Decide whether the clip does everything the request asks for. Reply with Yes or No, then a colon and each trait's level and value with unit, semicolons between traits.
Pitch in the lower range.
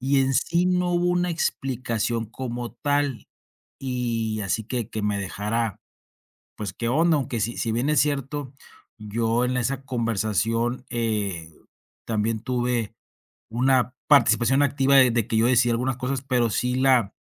Yes: low, 120 Hz